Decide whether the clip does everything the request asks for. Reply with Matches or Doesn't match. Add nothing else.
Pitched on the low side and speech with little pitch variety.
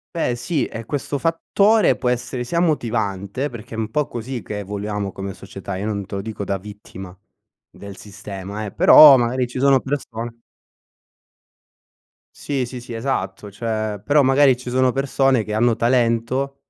Doesn't match